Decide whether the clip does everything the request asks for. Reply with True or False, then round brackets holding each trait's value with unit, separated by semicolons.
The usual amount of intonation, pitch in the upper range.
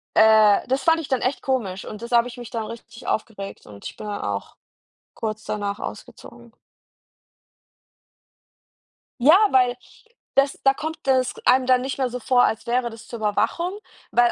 True (3.2 semitones; 240 Hz)